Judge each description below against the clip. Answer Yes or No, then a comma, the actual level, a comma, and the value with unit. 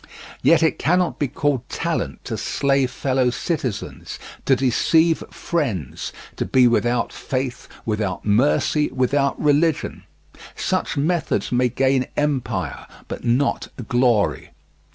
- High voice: No, low, 135 Hz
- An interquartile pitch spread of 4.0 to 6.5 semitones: No, average, 3.4 semitones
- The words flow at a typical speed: No, slow, 115 wpm